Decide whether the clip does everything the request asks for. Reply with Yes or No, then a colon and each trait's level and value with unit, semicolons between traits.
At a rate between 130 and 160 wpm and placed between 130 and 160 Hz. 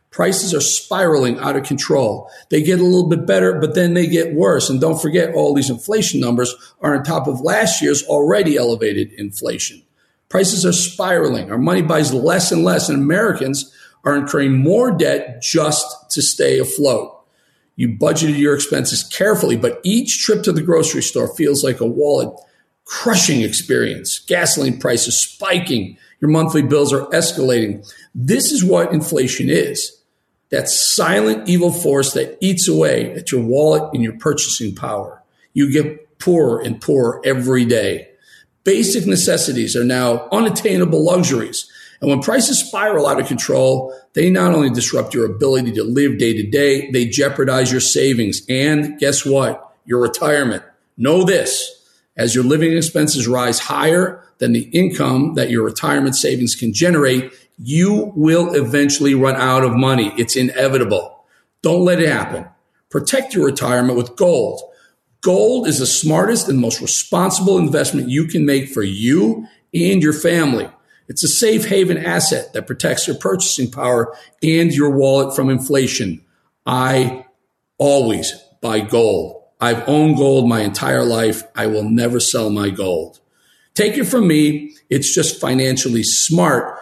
Yes: average, 155 wpm; medium, 140 Hz